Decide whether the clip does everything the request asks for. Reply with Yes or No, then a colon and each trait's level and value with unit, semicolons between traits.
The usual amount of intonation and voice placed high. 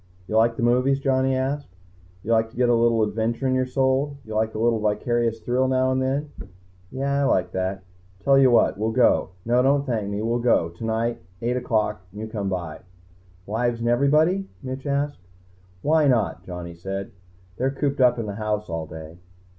No: average, 3.6 semitones; low, 120 Hz